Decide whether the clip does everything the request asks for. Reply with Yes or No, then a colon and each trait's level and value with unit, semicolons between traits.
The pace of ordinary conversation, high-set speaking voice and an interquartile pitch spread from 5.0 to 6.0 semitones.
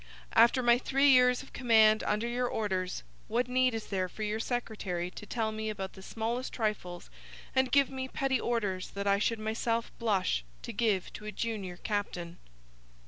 No: average, 180 wpm; high, 220 Hz; average, 3.4 semitones